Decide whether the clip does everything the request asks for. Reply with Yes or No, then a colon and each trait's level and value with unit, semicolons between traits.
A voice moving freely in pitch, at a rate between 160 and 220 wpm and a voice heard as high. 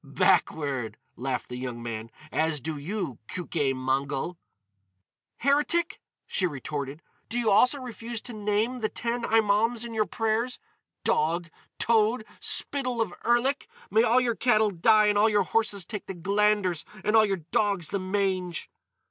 No: wide, 5.9 semitones; average, 150 wpm; high, 205 Hz